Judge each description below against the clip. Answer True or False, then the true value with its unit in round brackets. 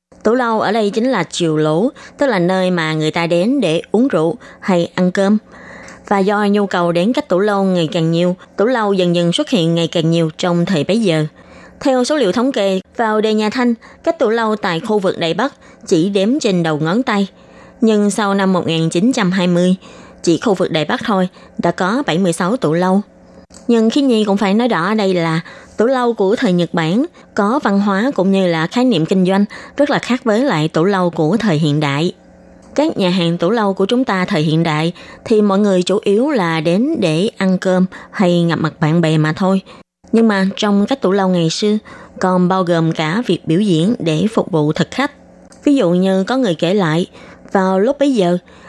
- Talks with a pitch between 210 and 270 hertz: False (190 Hz)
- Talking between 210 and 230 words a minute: True (220 wpm)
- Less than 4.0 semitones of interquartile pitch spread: False (4.6 semitones)